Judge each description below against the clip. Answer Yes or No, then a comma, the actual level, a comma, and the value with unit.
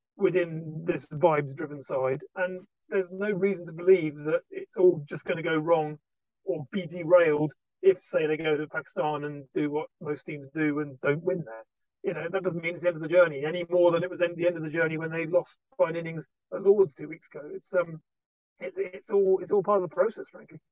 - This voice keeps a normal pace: No, fast, 230 wpm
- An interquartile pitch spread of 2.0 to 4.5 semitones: Yes, average, 3.2 semitones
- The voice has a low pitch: No, medium, 170 Hz